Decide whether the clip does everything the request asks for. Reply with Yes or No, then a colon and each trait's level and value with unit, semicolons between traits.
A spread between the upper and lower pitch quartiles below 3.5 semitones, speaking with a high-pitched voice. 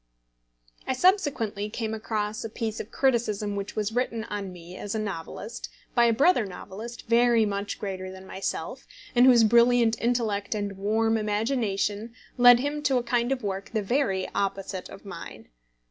Yes: average, 3.0 semitones; high, 220 Hz